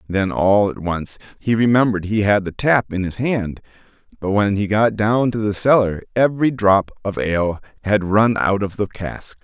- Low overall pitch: Yes, low, 105 Hz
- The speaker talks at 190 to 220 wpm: Yes, average, 195 wpm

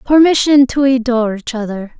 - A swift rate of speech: No, average, 150 wpm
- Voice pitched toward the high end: Yes, very high, 250 Hz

